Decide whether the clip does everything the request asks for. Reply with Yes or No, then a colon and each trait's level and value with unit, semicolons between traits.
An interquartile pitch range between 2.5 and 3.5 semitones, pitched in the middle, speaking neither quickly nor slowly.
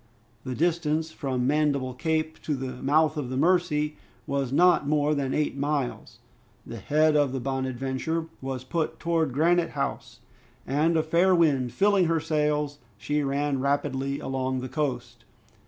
Yes: average, 3.0 semitones; medium, 145 Hz; average, 155 wpm